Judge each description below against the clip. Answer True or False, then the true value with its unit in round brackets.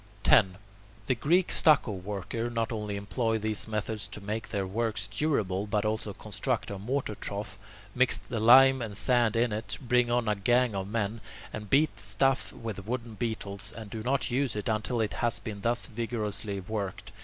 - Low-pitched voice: True (110 Hz)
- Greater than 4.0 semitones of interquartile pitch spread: False (2.8 semitones)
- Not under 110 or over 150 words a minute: False (185 wpm)